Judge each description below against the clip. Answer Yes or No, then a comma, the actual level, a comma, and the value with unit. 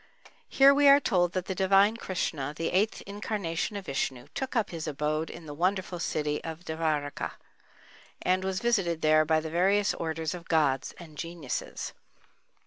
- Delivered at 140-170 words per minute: Yes, average, 160 wpm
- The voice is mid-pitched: Yes, medium, 170 Hz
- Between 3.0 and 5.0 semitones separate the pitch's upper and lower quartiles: Yes, average, 3.8 semitones